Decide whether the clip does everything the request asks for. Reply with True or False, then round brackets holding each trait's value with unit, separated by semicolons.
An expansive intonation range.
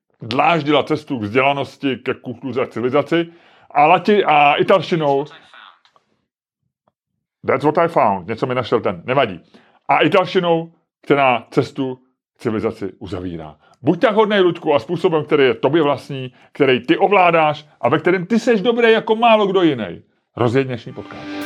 True (6.3 semitones)